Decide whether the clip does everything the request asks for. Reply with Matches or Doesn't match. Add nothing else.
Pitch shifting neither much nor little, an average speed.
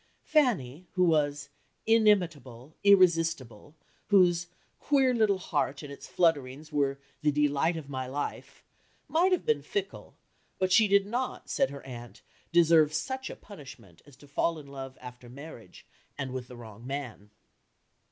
Doesn't match